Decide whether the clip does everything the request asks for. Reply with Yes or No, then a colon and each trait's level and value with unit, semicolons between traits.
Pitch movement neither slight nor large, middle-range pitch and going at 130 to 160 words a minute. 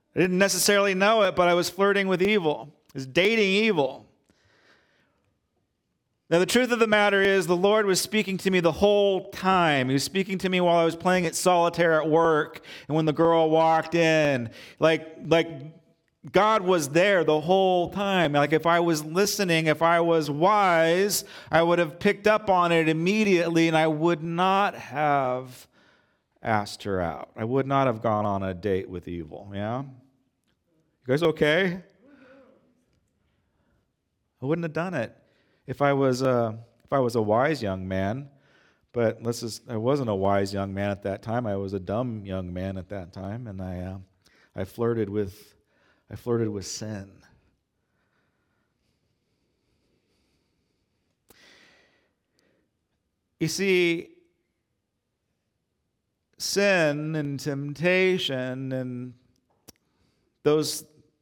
No: wide, 7.9 semitones; medium, 155 Hz; average, 145 wpm